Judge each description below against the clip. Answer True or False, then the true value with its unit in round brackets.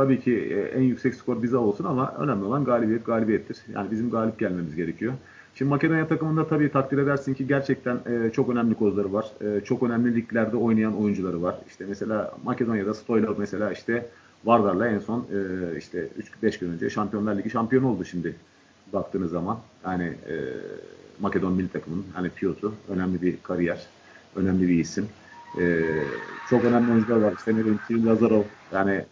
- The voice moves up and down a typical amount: True (3.9 semitones)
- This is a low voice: True (110 Hz)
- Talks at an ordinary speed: False (155 wpm)